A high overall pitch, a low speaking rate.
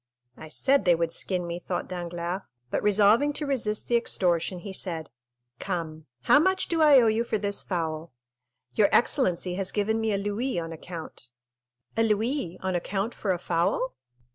No: high, 195 Hz; average, 175 wpm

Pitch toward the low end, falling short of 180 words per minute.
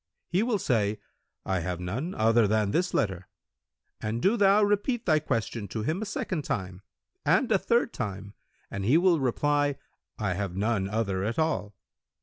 Yes: low, 115 Hz; average, 170 wpm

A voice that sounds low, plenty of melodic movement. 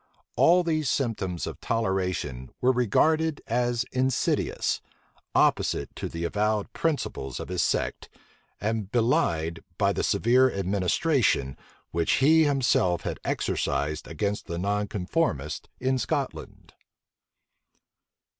Yes: low, 105 Hz; wide, 6.7 semitones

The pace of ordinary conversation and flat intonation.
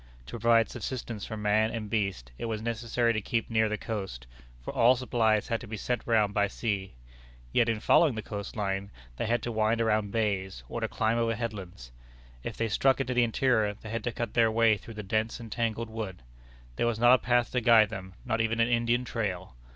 No: fast, 220 wpm; narrow, 2.1 semitones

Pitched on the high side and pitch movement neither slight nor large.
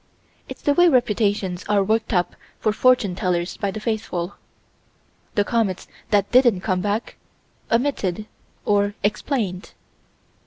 Yes: high, 205 Hz; average, 3.3 semitones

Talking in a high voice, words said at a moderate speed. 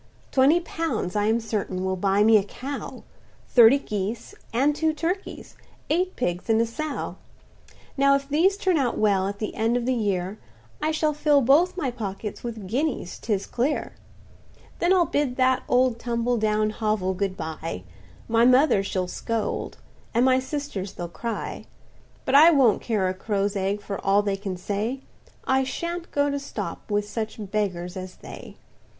Yes: high, 230 Hz; average, 170 wpm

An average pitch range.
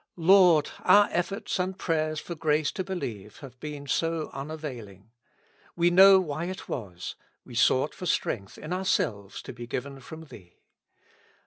No: wide, 6.0 semitones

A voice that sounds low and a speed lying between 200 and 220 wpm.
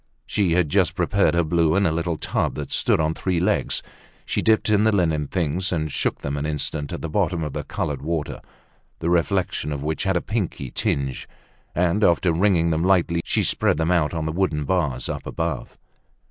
Yes: very low, 85 Hz; fast, 205 wpm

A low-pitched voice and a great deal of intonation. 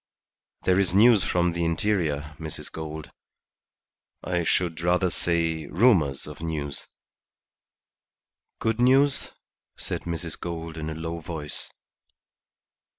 No: very low, 85 Hz; narrow, 2.5 semitones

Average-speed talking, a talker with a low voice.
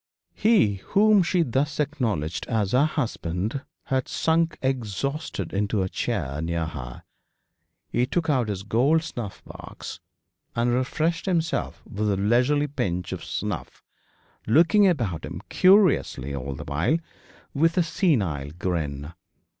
No: slow, 130 wpm; low, 120 Hz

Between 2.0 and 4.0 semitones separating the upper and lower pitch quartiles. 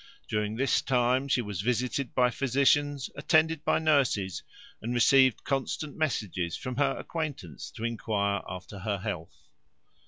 No: average, 5.1 semitones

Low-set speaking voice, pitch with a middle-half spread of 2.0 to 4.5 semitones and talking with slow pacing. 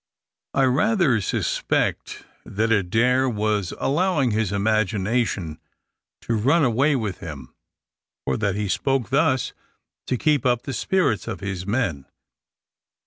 No: low, 115 Hz; average, 4.9 semitones; slow, 125 wpm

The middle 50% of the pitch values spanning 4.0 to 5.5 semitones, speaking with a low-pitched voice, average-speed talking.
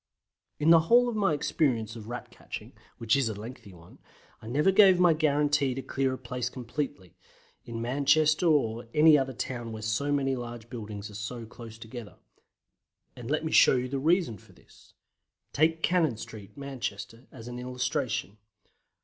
Yes: average, 4.7 semitones; low, 125 Hz; average, 170 wpm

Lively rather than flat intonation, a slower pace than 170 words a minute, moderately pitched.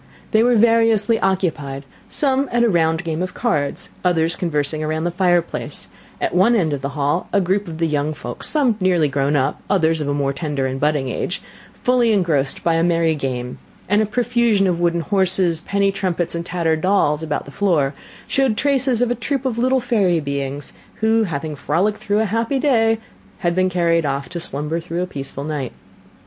No: wide, 6.1 semitones; average, 200 wpm; medium, 175 Hz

